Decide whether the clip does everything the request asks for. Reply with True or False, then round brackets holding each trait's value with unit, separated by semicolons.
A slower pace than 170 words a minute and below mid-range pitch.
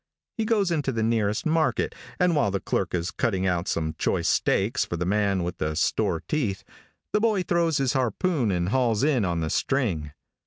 False (195 wpm; 110 Hz)